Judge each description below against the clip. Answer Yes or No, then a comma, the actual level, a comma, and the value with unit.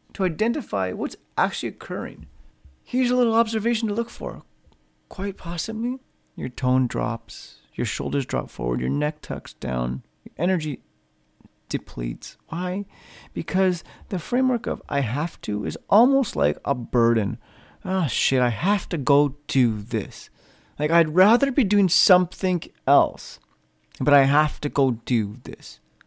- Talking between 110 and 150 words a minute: Yes, average, 145 wpm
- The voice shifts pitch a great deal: Yes, wide, 8.9 semitones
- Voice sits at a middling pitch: Yes, medium, 150 Hz